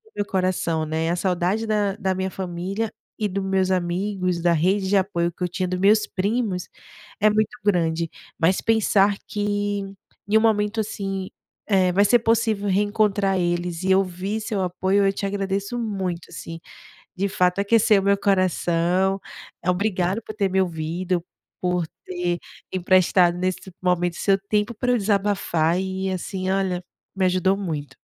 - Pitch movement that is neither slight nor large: No, narrow, 2.3 semitones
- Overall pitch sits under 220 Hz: Yes, high, 190 Hz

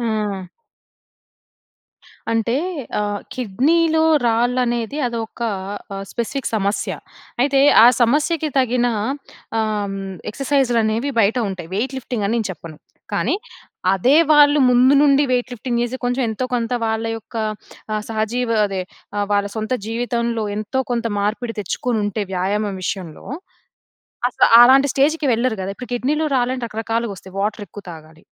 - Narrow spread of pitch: No, average, 3.5 semitones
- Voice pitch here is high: Yes, high, 230 Hz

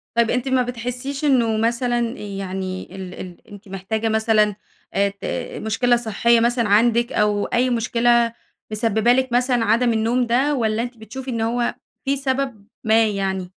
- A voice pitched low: No, high, 230 Hz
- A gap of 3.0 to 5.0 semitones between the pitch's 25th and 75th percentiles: No, narrow, 2.6 semitones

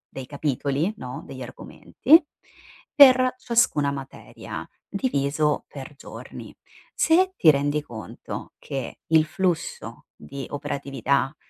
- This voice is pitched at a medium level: Yes, medium, 145 Hz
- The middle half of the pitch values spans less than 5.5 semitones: No, wide, 6.1 semitones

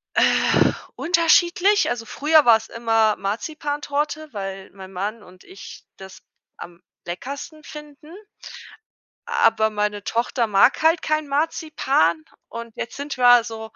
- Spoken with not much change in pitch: No, wide, 6.5 semitones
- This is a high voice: Yes, high, 235 Hz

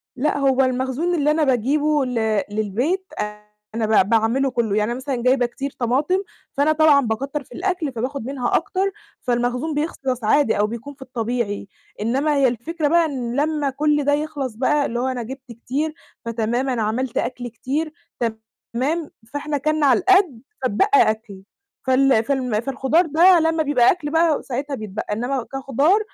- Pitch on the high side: Yes, very high, 265 Hz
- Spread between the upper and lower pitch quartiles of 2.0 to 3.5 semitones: No, average, 3.9 semitones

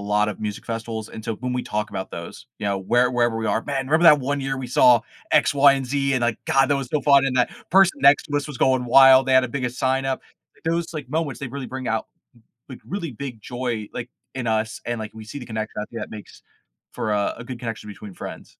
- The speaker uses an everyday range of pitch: Yes, average, 3.5 semitones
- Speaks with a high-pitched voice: No, low, 125 Hz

